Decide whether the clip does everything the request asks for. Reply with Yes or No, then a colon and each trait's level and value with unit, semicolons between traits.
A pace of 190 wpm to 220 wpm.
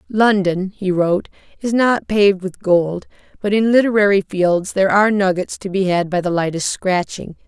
No: average, 175 wpm